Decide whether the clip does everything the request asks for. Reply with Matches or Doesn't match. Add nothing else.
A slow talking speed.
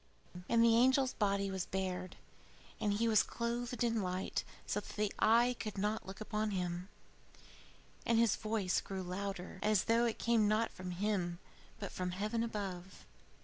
Doesn't match